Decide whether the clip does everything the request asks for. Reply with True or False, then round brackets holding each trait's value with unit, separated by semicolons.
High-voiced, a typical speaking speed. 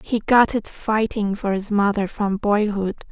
True (205 Hz; 175 wpm)